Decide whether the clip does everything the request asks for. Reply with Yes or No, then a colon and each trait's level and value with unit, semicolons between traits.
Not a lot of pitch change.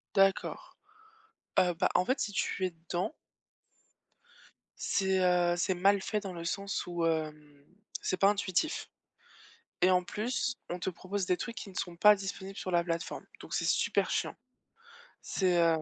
Yes: narrow, 2.3 semitones